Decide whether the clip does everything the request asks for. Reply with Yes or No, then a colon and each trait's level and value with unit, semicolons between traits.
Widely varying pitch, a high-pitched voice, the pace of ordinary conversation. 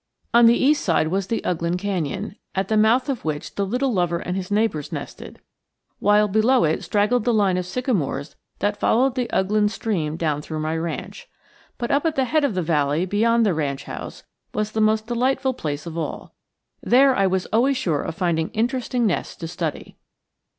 Yes: wide, 6.0 semitones; high, 205 Hz; average, 195 wpm